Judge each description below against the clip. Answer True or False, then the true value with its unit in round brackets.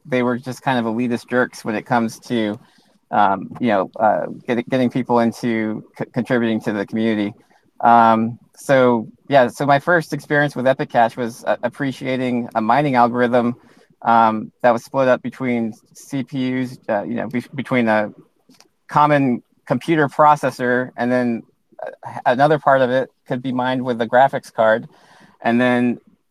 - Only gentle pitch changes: True (2.1 semitones)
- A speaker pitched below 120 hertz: False (125 Hz)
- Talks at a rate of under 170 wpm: True (160 wpm)